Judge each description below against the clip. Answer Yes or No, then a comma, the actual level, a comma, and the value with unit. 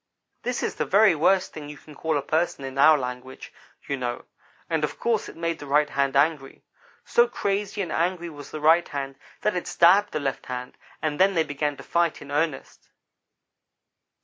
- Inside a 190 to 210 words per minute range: Yes, average, 200 wpm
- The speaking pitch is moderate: Yes, medium, 155 Hz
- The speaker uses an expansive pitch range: No, average, 3.7 semitones